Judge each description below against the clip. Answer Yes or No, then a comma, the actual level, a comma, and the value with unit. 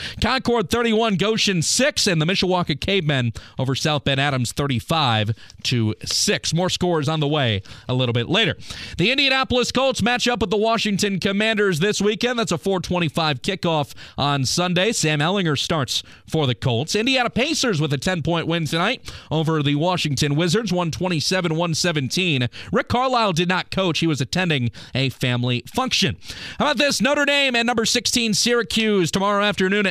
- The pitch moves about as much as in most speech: No, wide, 7.0 semitones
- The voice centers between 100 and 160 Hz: No, medium, 175 Hz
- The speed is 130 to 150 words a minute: No, average, 165 wpm